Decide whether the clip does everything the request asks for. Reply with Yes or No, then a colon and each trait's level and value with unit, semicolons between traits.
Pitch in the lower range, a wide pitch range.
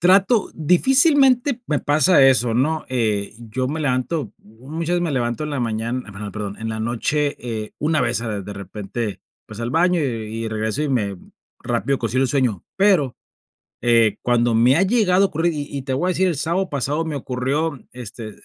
Yes: low, 130 Hz; wide, 6.1 semitones